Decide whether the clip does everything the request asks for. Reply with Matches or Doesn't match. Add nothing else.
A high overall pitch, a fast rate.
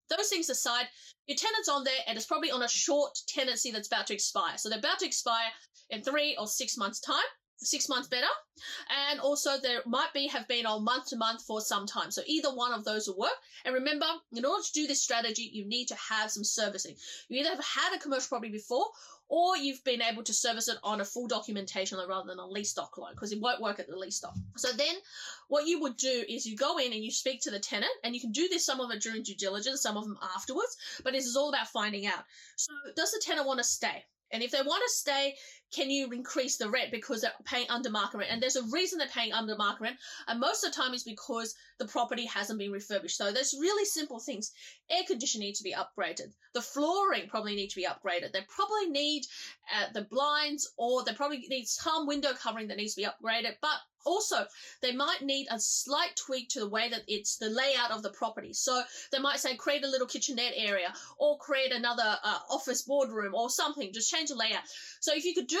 Matches